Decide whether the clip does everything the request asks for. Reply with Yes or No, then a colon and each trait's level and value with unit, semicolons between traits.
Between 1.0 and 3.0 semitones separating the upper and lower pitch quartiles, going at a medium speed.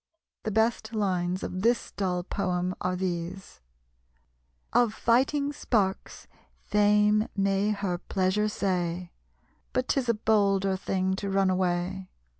No: narrow, 2.5 semitones; slow, 120 wpm